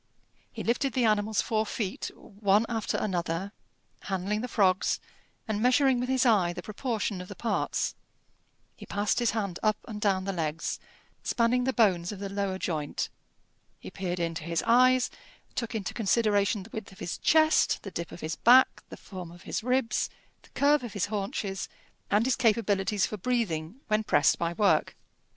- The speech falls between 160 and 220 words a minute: Yes, average, 175 wpm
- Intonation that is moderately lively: Yes, average, 3.7 semitones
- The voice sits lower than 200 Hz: No, high, 210 Hz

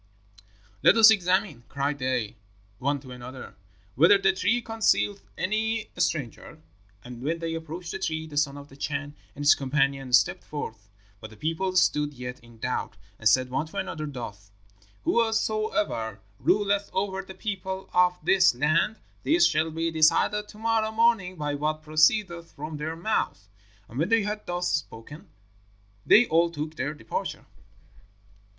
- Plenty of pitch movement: Yes, wide, 6.0 semitones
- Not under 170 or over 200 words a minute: No, average, 155 wpm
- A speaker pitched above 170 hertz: No, medium, 160 Hz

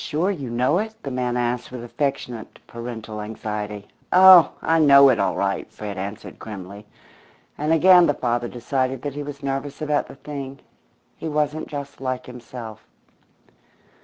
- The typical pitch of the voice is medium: No, low, 130 Hz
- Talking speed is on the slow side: No, average, 160 wpm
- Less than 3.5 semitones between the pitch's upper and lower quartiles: No, average, 3.9 semitones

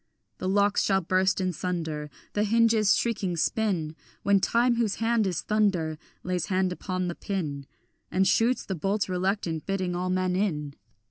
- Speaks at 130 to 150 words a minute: No, average, 160 wpm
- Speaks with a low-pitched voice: No, high, 190 Hz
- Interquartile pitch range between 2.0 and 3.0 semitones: Yes, narrow, 2.6 semitones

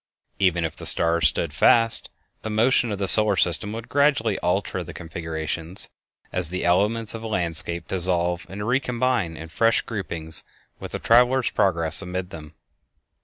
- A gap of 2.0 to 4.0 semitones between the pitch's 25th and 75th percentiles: No, average, 5.0 semitones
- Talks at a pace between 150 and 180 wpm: Yes, average, 160 wpm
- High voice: No, very low, 95 Hz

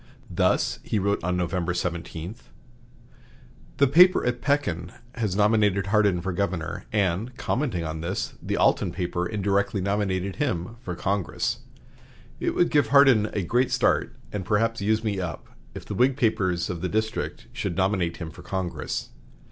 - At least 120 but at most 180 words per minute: Yes, average, 155 wpm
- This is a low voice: Yes, low, 100 Hz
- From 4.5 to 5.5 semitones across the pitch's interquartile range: No, average, 3.8 semitones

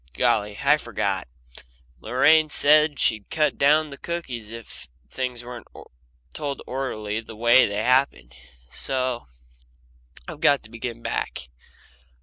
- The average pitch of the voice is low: Yes, low, 125 Hz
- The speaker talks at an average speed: No, slow, 125 wpm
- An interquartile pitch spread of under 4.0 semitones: No, average, 4.5 semitones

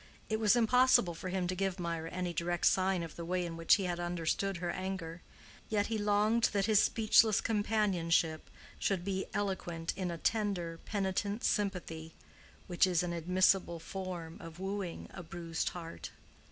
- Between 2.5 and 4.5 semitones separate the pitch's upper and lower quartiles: Yes, average, 3.0 semitones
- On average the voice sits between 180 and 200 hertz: Yes, medium, 185 Hz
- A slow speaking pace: No, average, 165 wpm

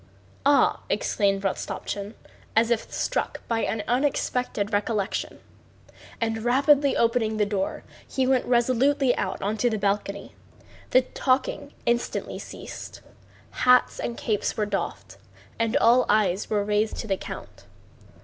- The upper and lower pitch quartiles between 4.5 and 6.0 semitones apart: No, average, 3.4 semitones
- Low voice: No, high, 225 Hz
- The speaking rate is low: Yes, slow, 130 wpm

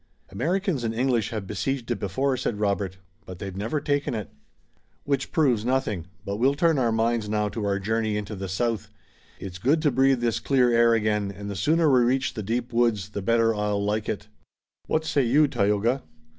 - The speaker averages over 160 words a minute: Yes, average, 200 wpm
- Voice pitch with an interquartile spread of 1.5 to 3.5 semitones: No, average, 4.3 semitones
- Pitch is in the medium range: No, low, 115 Hz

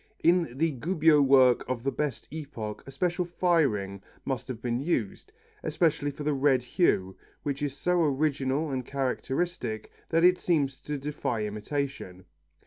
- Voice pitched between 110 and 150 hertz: Yes, medium, 140 Hz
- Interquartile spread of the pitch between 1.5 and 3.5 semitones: No, average, 4.1 semitones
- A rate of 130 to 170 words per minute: Yes, average, 150 wpm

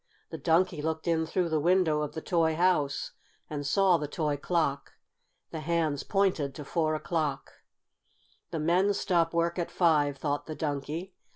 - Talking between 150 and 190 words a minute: Yes, average, 165 wpm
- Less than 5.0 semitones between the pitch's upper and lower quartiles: Yes, narrow, 2.5 semitones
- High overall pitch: No, medium, 160 Hz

